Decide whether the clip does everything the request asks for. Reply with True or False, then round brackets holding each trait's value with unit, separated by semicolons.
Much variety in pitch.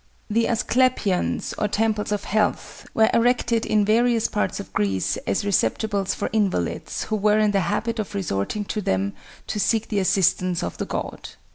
False (2.8 semitones)